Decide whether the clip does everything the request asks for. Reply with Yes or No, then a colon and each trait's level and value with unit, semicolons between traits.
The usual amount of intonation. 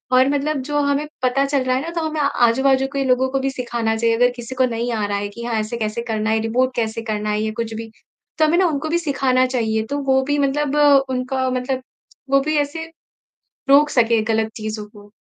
Yes: average, 3.6 semitones